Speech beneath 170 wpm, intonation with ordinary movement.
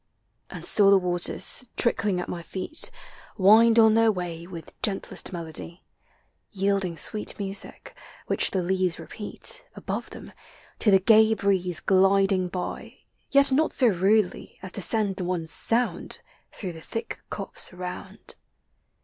Yes: average, 140 wpm; average, 3.3 semitones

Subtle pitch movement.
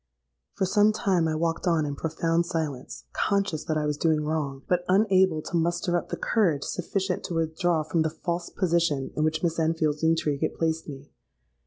Yes: narrow, 2.2 semitones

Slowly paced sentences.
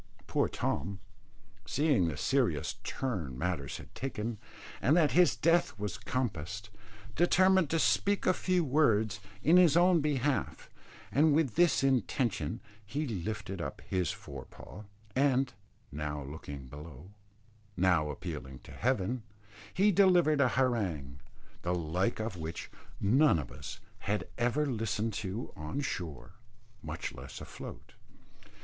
Yes: slow, 130 wpm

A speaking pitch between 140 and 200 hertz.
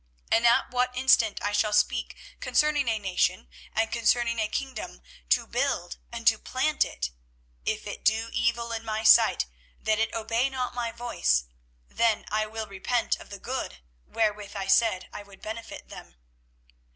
No: high, 225 Hz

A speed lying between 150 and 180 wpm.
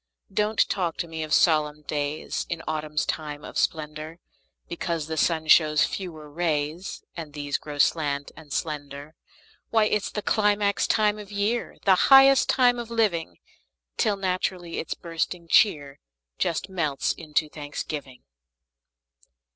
No: average, 140 wpm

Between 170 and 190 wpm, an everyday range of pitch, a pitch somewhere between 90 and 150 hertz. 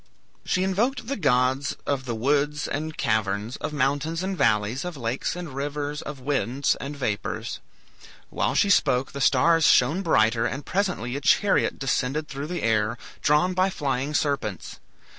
No: average, 160 wpm; average, 4.4 semitones; medium, 140 Hz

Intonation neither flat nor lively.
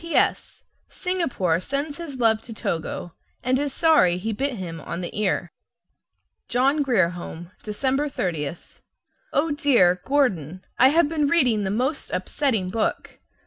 No: wide, 7.8 semitones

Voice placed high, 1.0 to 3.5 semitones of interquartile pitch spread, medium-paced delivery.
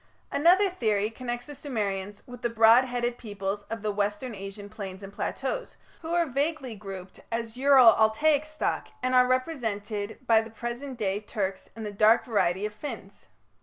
No: high, 225 Hz; average, 3.9 semitones; average, 170 wpm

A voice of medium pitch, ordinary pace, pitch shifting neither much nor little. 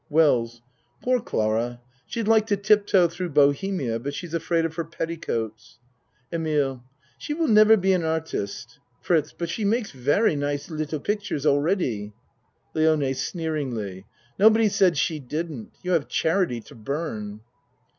No: medium, 160 Hz; average, 145 wpm; wide, 5.8 semitones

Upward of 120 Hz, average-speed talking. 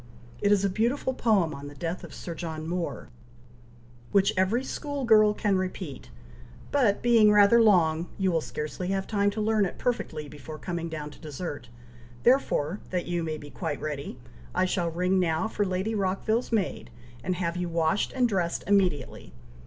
Yes: medium, 185 Hz; average, 175 wpm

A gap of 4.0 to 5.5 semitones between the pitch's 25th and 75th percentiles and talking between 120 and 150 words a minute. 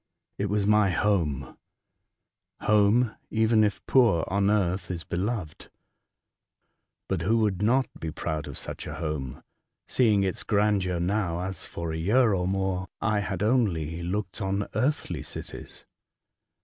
No: average, 3.5 semitones; average, 140 wpm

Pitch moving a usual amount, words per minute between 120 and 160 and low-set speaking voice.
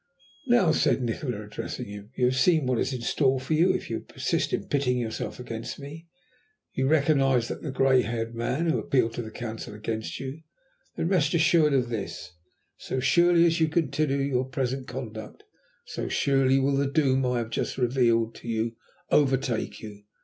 No: average, 3.7 semitones; average, 185 wpm; low, 130 Hz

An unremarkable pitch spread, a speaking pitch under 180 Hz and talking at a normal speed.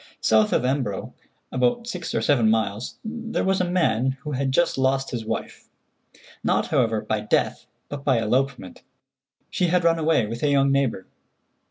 No: wide, 6.3 semitones; low, 135 Hz; average, 165 wpm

